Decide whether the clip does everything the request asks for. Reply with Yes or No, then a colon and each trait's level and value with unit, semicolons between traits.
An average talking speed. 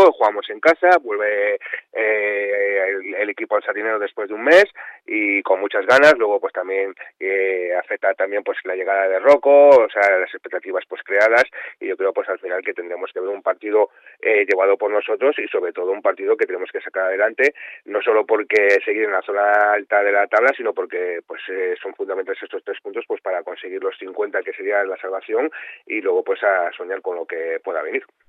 No: fast, 210 wpm